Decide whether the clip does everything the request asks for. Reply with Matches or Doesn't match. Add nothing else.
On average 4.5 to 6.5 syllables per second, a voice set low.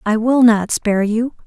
Doesn't match